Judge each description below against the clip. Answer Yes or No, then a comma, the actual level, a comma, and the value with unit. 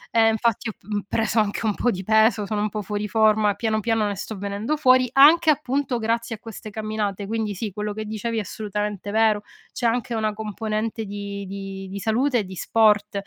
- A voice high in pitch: Yes, high, 215 Hz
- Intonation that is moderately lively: No, narrow, 1.7 semitones